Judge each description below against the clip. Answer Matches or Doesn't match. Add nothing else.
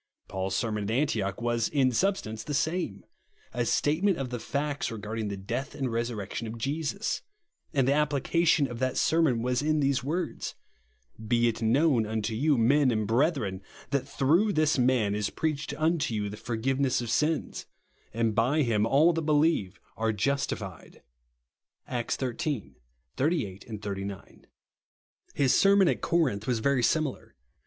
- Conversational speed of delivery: Matches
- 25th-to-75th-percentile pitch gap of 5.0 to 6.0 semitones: Matches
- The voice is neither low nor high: Doesn't match